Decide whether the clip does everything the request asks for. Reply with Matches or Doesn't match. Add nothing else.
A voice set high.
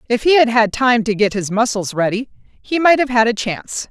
Matches